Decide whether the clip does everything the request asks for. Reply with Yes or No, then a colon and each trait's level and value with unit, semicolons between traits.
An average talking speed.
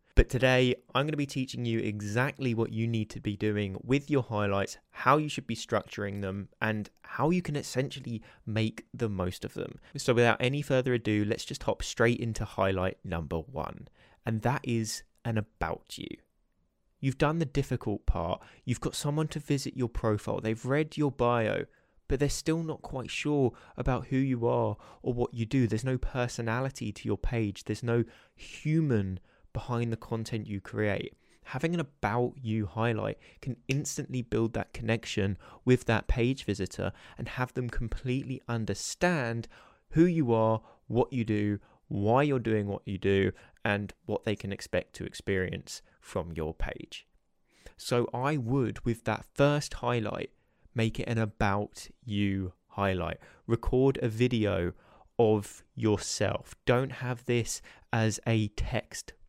Yes: average, 165 wpm